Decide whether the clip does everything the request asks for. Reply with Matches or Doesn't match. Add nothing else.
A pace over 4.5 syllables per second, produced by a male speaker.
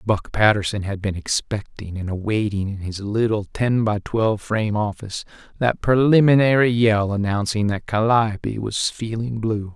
Matches